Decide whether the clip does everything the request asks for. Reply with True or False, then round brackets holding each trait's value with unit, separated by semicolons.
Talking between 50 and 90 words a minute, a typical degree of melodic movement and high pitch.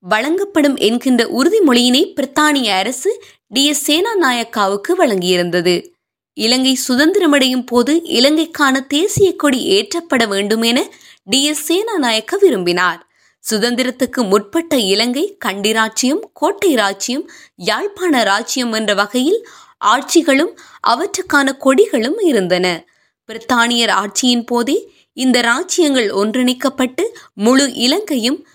False (85 wpm; 6.5 semitones; 265 Hz)